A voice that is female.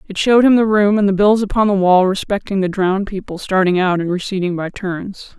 Yes: female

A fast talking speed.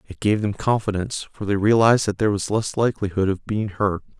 Yes: fast, 215 wpm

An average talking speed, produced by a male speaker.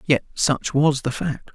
Yes: average, 195 wpm; male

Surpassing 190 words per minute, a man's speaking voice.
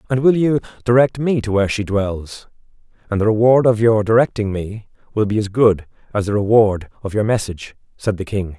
Yes: fast, 205 wpm; male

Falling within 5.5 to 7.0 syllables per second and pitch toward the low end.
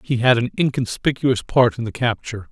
Yes: 5.6 syllables/s; low, 120 Hz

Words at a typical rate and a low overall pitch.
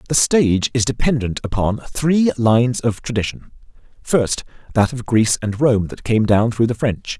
Yes: average, 175 wpm; low, 120 Hz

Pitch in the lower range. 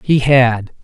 Yes: low, 125 Hz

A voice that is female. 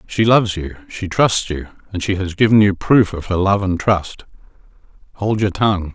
No: male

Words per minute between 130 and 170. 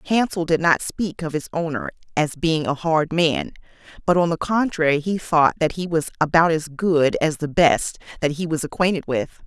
No: fast, 205 wpm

